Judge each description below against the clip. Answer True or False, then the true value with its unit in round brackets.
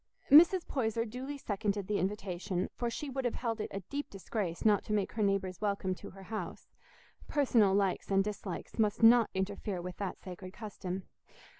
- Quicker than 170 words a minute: True (180 wpm)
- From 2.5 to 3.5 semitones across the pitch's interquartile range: True (3.2 semitones)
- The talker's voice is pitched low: False (205 Hz)